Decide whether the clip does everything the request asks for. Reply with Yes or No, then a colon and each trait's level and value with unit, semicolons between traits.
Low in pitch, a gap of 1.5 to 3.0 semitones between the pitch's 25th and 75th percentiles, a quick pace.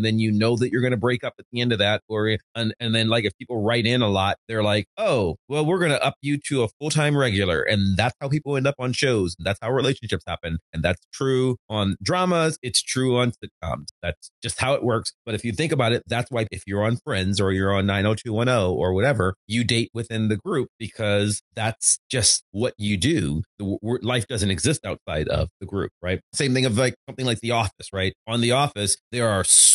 No: low, 115 Hz; average, 3.7 semitones; fast, 245 wpm